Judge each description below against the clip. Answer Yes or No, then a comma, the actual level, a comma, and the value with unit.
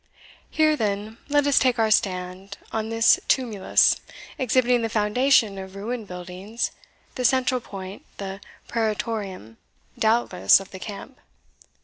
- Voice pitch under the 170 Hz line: No, high, 220 Hz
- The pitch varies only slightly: No, average, 3.9 semitones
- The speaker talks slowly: Yes, slow, 125 wpm